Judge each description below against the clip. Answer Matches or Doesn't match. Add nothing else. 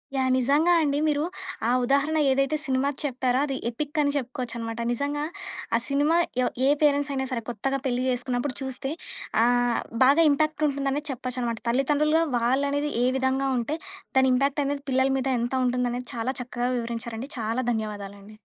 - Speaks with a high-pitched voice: Matches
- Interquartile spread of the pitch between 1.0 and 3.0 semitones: Matches